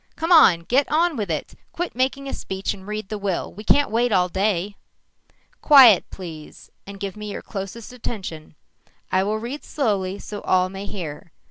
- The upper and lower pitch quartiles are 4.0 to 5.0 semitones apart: Yes, average, 4.6 semitones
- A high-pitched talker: Yes, high, 205 Hz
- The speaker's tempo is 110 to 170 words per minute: No, average, 180 wpm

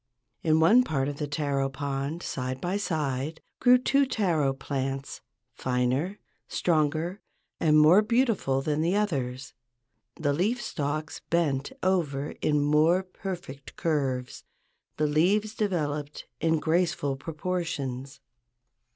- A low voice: No, medium, 155 Hz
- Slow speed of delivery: Yes, slow, 115 wpm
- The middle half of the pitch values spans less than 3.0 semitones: No, average, 4.5 semitones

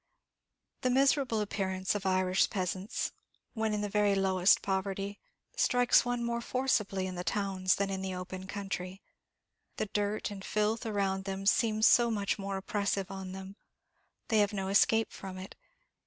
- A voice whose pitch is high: Yes, high, 200 Hz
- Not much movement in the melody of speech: Yes, narrow, 2.0 semitones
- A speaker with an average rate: Yes, average, 160 wpm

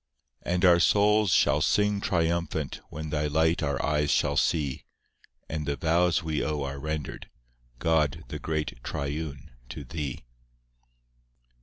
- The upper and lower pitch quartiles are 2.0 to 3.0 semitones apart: Yes, narrow, 2.6 semitones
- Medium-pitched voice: No, very low, 75 Hz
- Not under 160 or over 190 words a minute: No, average, 140 wpm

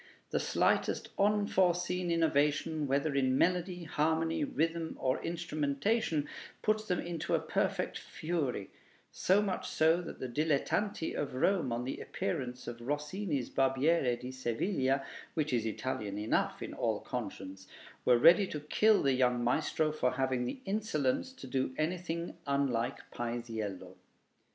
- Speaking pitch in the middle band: Yes, medium, 150 Hz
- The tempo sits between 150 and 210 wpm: No, slow, 135 wpm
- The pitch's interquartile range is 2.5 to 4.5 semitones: No, average, 5.3 semitones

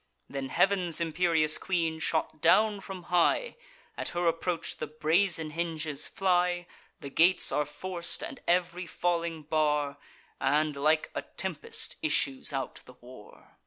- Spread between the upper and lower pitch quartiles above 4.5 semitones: No, average, 2.8 semitones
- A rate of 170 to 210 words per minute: No, slow, 135 wpm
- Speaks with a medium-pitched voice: Yes, medium, 165 Hz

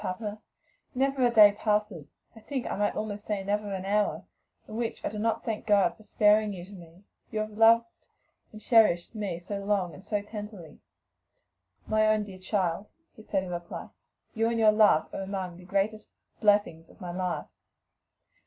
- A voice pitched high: Yes, high, 210 Hz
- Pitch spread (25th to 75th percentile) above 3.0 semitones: No, narrow, 2.5 semitones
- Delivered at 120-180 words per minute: No, average, 190 wpm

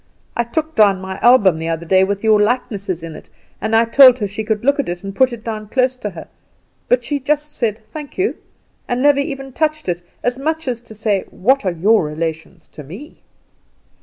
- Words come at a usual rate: No, fast, 220 wpm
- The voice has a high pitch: Yes, high, 225 Hz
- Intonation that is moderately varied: No, wide, 6.0 semitones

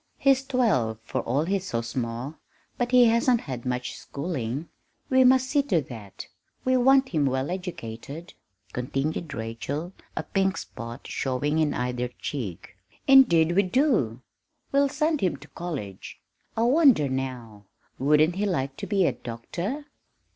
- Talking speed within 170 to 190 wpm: No, average, 145 wpm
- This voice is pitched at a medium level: Yes, medium, 155 Hz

